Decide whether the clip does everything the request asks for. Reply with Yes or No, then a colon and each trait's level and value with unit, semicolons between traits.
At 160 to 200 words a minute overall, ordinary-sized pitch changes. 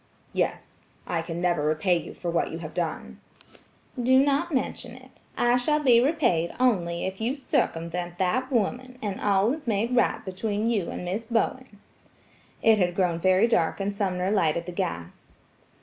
No: average, 170 wpm; wide, 6.0 semitones